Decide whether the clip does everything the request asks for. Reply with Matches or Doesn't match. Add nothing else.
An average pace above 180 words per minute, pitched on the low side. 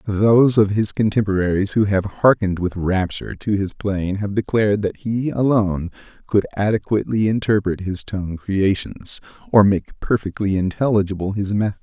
Doesn't match